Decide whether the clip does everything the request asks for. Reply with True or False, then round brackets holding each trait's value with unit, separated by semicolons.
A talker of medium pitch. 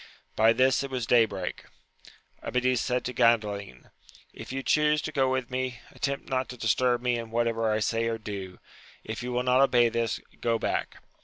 False (120 Hz)